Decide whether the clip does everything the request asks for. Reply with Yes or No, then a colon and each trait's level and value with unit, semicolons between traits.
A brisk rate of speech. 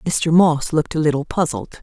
No: average, 195 wpm